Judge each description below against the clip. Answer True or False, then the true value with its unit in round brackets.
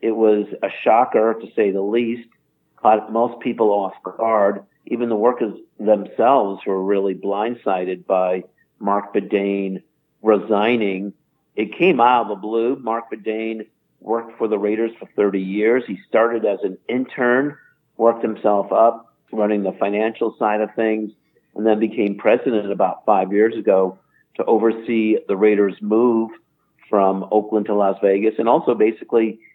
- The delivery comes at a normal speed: True (150 wpm)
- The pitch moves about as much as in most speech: False (2.2 semitones)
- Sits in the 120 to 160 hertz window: False (110 Hz)